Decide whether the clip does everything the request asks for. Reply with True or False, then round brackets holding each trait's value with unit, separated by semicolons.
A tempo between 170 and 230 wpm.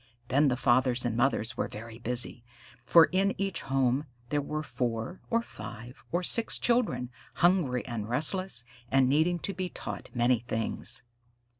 False (155 wpm)